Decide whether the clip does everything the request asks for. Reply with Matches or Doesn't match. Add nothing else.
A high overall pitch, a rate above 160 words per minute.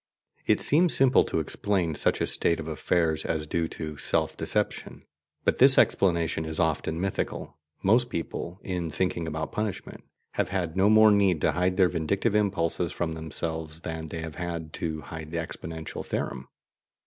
Doesn't match